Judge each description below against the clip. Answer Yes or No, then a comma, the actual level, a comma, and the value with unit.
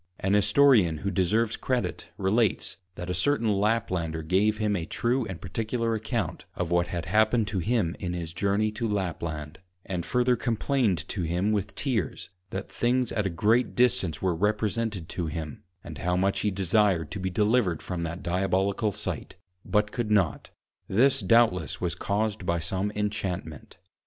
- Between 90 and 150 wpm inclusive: No, average, 165 wpm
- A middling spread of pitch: Yes, average, 3.9 semitones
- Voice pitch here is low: Yes, low, 100 Hz